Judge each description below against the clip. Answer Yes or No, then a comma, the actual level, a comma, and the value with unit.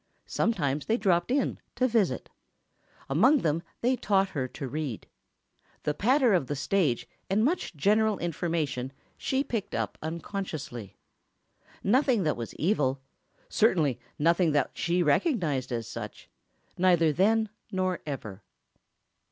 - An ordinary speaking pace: No, slow, 120 wpm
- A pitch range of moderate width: No, wide, 6.9 semitones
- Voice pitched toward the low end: No, medium, 170 Hz